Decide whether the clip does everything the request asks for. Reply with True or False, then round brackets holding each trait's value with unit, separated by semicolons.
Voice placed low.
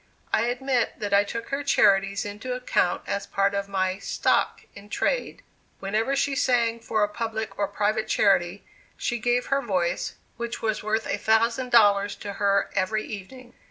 False (215 Hz)